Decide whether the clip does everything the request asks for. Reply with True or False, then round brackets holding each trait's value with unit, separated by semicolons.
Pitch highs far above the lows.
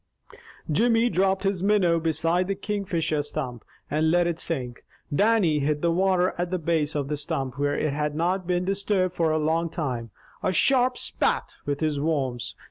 False (4.0 semitones)